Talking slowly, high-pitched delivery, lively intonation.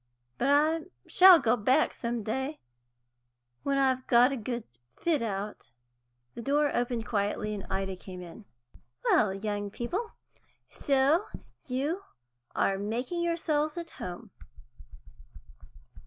Yes: slow, 120 wpm; very high, 250 Hz; wide, 6.0 semitones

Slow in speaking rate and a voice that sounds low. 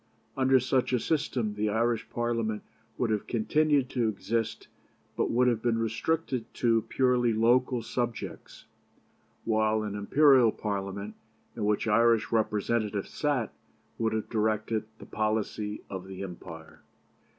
Yes: slow, 130 wpm; low, 115 Hz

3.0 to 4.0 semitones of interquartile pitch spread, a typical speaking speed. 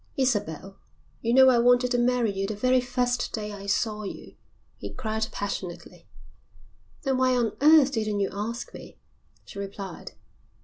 Yes: average, 3.7 semitones; average, 160 wpm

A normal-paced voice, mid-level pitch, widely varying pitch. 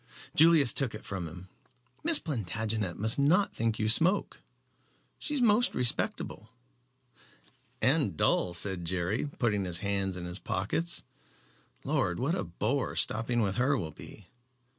No: average, 145 wpm; low, 110 Hz; wide, 7.0 semitones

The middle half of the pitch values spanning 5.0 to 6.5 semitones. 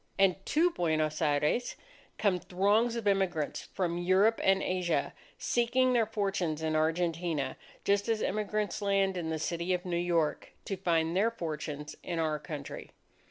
No: average, 4.0 semitones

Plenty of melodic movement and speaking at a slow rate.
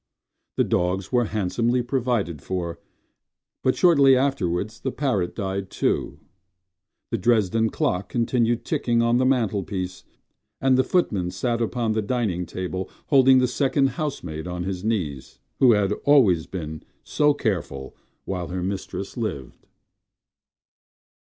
Yes: wide, 5.8 semitones; slow, 130 wpm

